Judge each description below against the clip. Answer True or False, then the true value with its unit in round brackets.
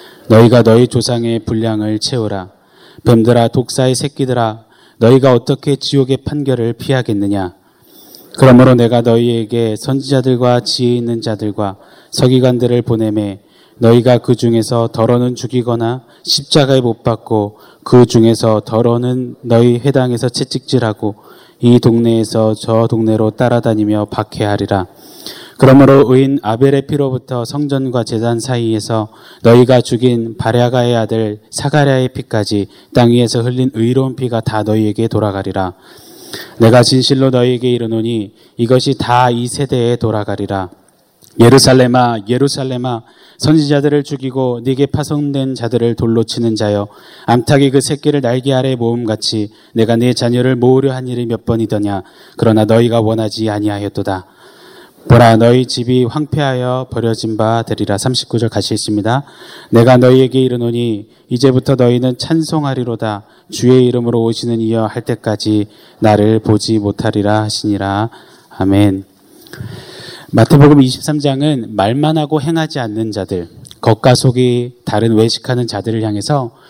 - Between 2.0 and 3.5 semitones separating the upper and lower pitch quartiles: True (2.7 semitones)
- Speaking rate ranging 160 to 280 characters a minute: False (315 characters per minute)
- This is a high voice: False (120 Hz)